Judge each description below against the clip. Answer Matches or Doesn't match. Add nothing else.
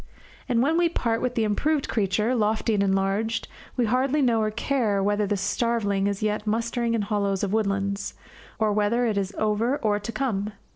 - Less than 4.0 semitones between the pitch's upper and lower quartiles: Matches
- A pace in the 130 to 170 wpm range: Doesn't match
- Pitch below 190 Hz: Doesn't match